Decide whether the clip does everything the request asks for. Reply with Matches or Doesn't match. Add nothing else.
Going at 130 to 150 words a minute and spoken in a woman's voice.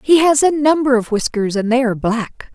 Doesn't match